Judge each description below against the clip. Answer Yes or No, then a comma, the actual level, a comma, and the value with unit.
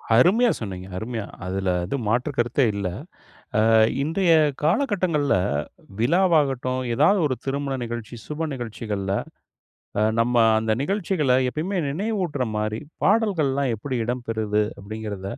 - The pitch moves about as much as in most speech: No, wide, 6.7 semitones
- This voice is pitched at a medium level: No, low, 130 Hz